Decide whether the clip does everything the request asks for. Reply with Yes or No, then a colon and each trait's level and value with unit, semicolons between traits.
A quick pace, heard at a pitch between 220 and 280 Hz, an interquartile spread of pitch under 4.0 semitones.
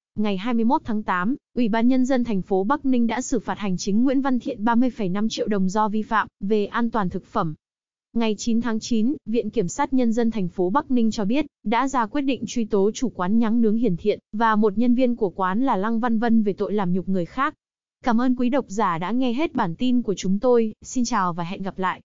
Yes: fast, 255 wpm; high, 225 Hz; average, 3.4 semitones